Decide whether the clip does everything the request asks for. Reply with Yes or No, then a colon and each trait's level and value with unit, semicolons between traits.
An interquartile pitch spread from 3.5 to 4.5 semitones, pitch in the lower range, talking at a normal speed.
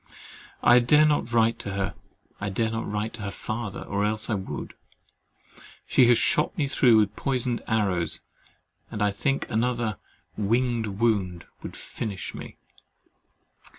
No: average, 2.9 semitones; low, 110 Hz; average, 150 wpm